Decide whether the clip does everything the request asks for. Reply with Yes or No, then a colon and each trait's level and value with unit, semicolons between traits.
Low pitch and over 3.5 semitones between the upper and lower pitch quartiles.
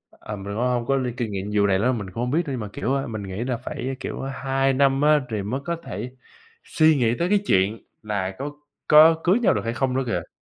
Yes: low, 125 Hz; average, 4.6 semitones